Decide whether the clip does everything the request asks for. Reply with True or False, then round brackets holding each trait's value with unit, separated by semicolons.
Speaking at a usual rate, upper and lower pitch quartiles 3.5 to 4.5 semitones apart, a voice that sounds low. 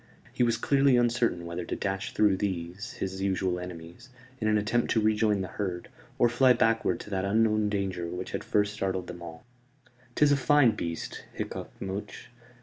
True (180 wpm; 3.8 semitones; 100 Hz)